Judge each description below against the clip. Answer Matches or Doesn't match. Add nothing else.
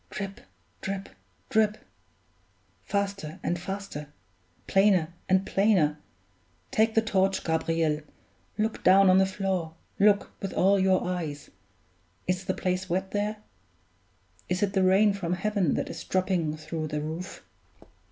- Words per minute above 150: Doesn't match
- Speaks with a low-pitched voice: Doesn't match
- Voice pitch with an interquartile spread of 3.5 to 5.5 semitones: Doesn't match